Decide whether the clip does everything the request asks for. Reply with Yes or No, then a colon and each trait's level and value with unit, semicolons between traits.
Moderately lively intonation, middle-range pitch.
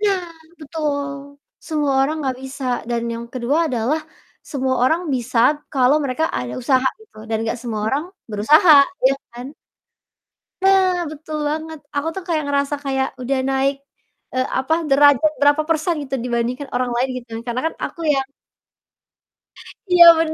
No: average, 3.6 semitones; very high, 275 Hz